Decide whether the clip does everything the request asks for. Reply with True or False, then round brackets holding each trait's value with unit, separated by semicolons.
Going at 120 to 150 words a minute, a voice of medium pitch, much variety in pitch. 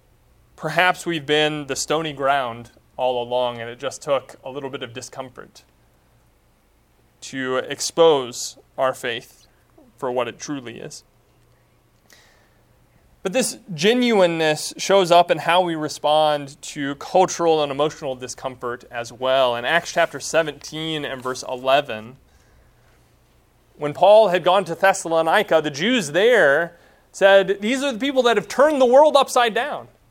True (140 wpm; 150 Hz; 5.9 semitones)